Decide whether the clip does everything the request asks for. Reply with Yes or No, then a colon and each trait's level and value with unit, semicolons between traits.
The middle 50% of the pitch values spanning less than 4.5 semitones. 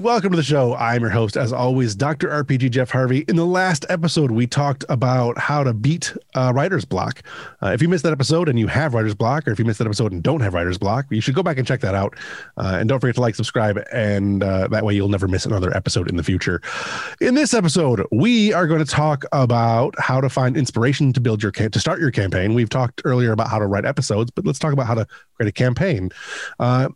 No: average, 5.0 semitones